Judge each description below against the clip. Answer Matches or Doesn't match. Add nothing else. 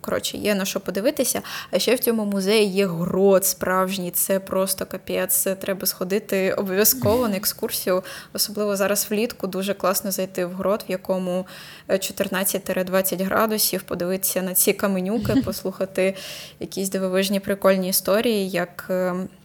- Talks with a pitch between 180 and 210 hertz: Matches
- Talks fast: Doesn't match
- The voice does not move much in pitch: Matches